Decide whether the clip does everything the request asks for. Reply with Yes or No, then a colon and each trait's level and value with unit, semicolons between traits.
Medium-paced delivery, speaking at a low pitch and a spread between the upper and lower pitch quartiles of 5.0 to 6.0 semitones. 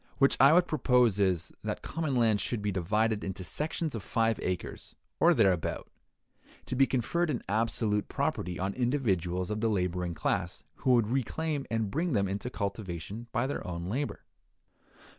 Yes: average, 165 wpm; low, 110 Hz; average, 5.3 semitones